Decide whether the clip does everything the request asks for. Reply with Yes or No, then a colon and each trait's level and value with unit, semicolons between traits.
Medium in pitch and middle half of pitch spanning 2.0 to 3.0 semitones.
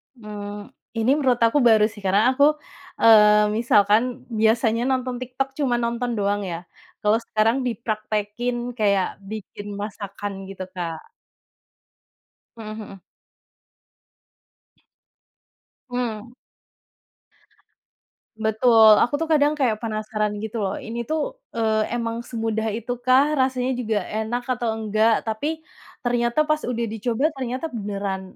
No: high, 225 Hz; narrow, 2.5 semitones